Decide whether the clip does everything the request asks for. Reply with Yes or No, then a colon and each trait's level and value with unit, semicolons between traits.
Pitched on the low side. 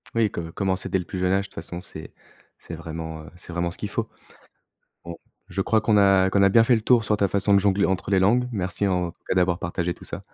Yes: very low, 95 Hz